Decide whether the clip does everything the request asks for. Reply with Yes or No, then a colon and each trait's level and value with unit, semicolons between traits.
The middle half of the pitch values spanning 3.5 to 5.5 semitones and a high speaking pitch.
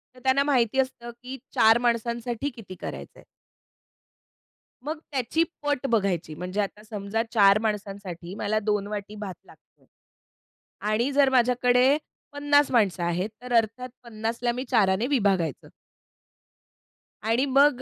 Yes: average, 4.1 semitones; high, 230 Hz